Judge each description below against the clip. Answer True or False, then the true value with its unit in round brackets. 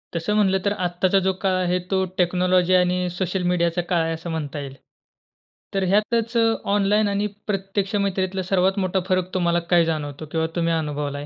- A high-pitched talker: False (180 Hz)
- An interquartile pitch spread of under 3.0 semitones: True (2.6 semitones)